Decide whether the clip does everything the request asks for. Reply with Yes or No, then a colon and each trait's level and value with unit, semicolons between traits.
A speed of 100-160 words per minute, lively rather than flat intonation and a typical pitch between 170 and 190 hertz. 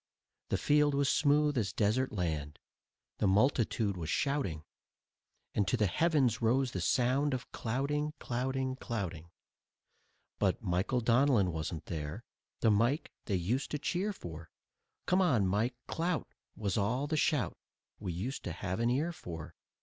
No: average, 150 wpm; wide, 6.9 semitones; low, 120 Hz